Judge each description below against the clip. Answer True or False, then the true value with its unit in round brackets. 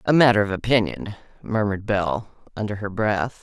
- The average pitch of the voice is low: True (105 Hz)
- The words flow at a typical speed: True (160 wpm)